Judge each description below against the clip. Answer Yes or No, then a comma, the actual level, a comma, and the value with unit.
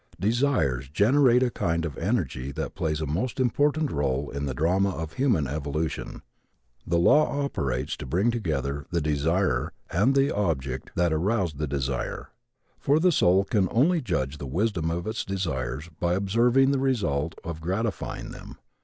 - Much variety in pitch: Yes, wide, 8.2 semitones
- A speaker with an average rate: Yes, average, 160 wpm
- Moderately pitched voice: No, very low, 85 Hz